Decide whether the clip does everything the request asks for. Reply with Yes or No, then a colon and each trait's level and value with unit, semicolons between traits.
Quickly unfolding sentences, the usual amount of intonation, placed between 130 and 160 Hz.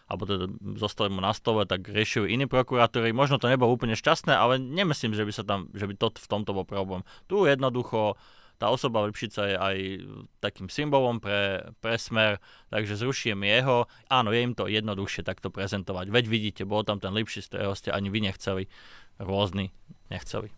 No: fast, 185 wpm; average, 3.2 semitones; low, 105 Hz